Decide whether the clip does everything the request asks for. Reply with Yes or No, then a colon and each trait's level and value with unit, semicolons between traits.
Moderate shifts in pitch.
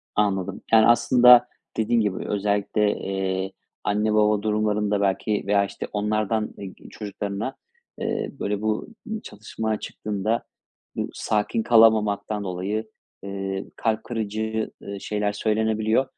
No: narrow, 1.5 semitones